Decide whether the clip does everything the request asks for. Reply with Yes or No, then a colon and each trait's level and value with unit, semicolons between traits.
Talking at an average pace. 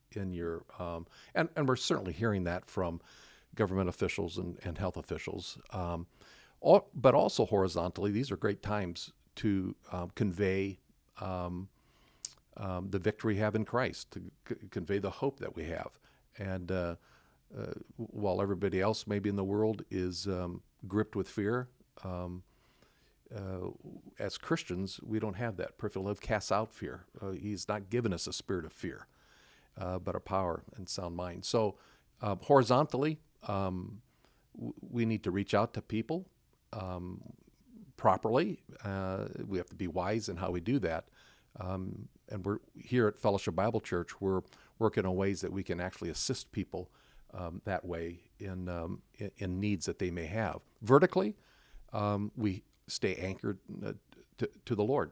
Yes: average, 165 wpm